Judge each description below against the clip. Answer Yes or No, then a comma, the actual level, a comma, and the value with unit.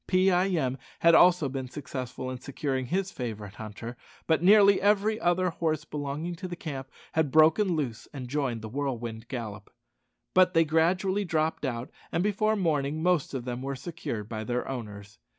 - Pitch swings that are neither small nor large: No, wide, 6.0 semitones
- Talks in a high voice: No, medium, 145 Hz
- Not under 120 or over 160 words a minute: No, average, 180 wpm